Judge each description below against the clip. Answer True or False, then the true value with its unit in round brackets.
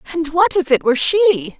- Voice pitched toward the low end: False (315 Hz)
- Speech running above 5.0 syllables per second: True (5.3 syllables/s)